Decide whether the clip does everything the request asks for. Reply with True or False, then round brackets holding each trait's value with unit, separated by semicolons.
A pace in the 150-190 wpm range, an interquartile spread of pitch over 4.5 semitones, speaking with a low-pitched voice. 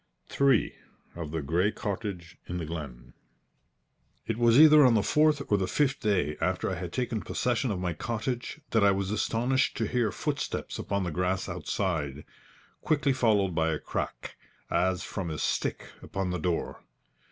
True (170 wpm; 5.4 semitones; 100 Hz)